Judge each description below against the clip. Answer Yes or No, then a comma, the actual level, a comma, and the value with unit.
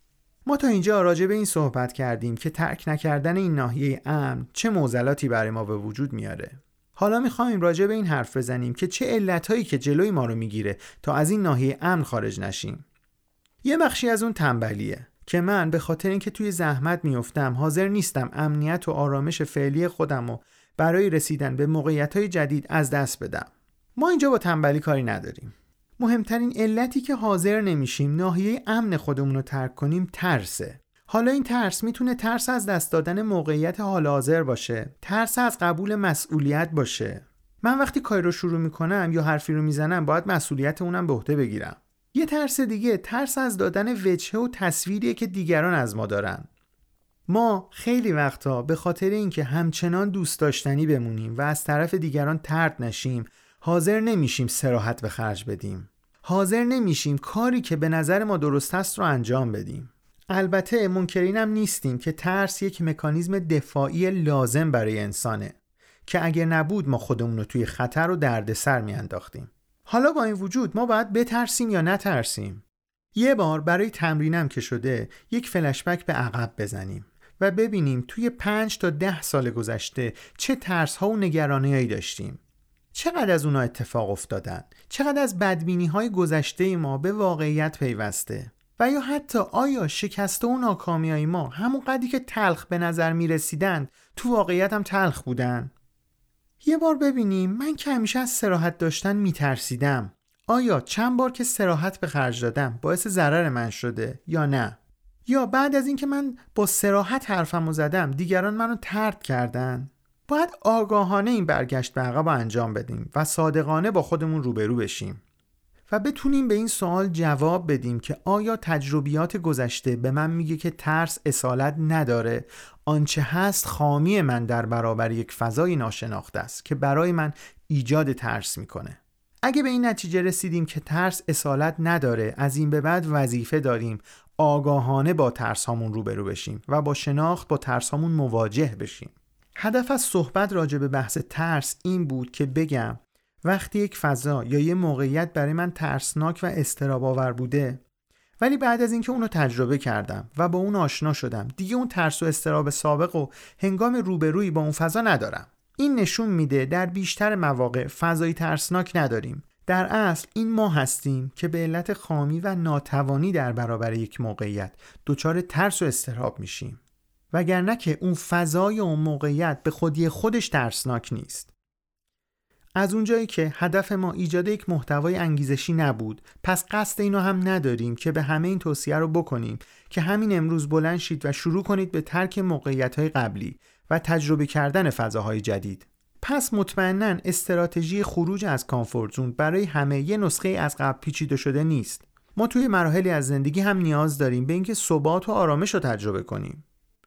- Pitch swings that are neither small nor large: No, wide, 6.2 semitones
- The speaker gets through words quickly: Yes, fast, 165 wpm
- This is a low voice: No, medium, 160 Hz